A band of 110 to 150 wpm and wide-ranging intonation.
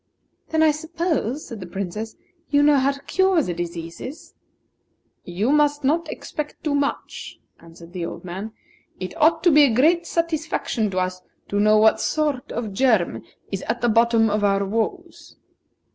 No: average, 170 wpm; wide, 7.1 semitones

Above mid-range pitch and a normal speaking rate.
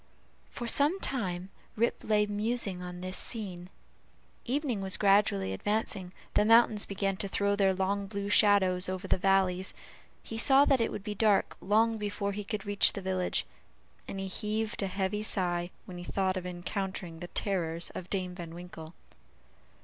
Yes: high, 195 Hz; average, 170 wpm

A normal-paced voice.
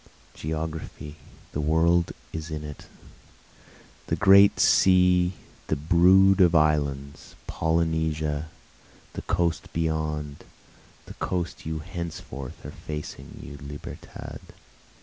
No: slow, 100 wpm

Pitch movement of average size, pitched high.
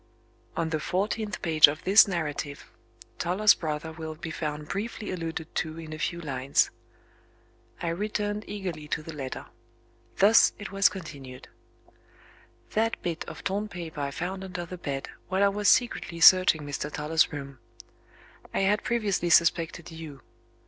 No: average, 4.3 semitones; medium, 170 Hz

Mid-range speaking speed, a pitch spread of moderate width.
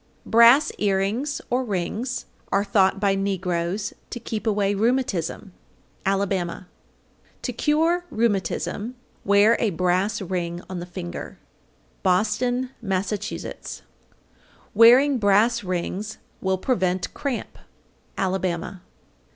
No: slow, 105 wpm; average, 3.8 semitones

